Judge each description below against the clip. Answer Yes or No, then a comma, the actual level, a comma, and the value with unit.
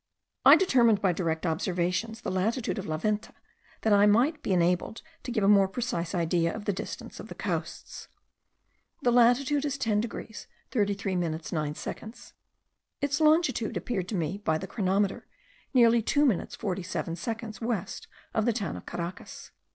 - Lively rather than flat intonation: No, average, 4.7 semitones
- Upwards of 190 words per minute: No, average, 165 wpm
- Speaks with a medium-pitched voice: No, high, 205 Hz